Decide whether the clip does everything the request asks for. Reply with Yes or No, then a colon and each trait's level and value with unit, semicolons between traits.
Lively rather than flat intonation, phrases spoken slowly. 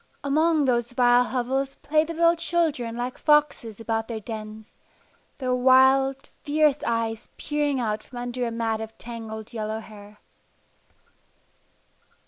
No: average, 3.9 semitones; slow, 130 wpm